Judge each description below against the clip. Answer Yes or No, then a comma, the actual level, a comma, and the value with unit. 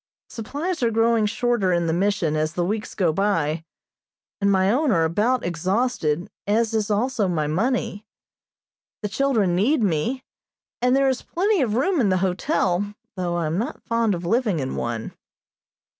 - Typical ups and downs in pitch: No, wide, 5.7 semitones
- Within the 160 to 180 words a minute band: Yes, average, 170 wpm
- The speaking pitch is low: No, high, 205 Hz